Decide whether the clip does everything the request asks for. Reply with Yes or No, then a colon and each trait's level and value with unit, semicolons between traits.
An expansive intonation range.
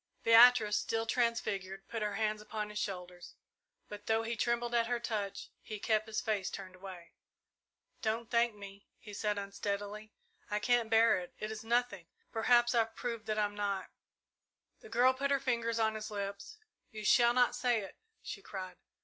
No: narrow, 2.5 semitones